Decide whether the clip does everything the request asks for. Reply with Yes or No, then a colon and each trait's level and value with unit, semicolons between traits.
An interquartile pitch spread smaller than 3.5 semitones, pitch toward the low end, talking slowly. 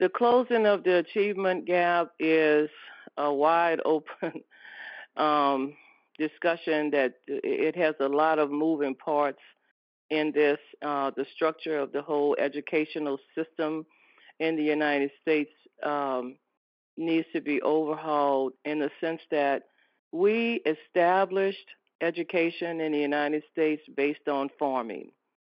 No: narrow, 2.4 semitones; medium, 155 Hz; slow, 125 wpm